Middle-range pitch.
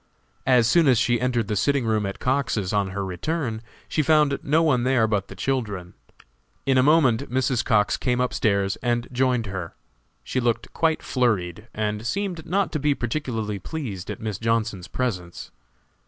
No: low, 120 Hz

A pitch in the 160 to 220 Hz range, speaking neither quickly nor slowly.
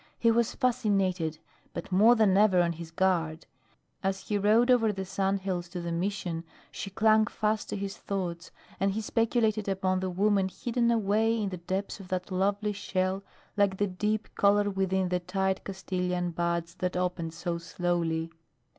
Yes: high, 190 Hz; average, 170 wpm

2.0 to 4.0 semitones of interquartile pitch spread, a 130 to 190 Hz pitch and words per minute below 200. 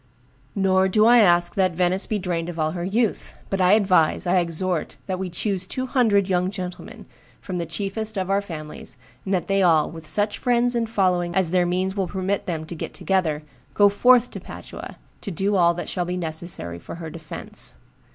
No: narrow, 2.6 semitones; medium, 185 Hz; fast, 205 wpm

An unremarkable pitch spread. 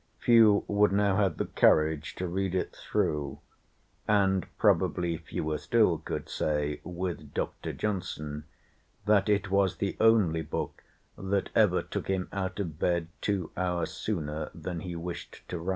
Yes: average, 3.7 semitones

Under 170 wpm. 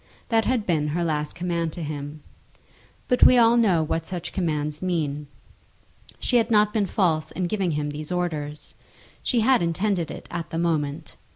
No: average, 175 wpm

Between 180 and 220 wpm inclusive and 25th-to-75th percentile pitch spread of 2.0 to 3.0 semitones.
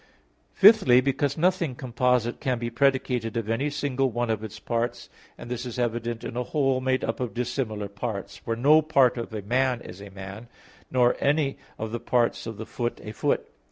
Yes: average, 195 wpm; average, 2.7 semitones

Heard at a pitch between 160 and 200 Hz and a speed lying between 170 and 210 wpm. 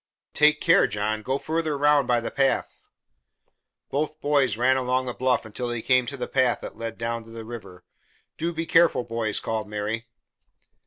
No: low, 125 Hz; average, 190 wpm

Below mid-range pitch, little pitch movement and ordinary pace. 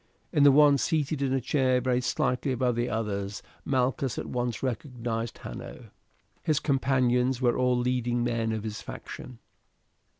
Yes: low, 125 Hz; narrow, 2.0 semitones; average, 155 wpm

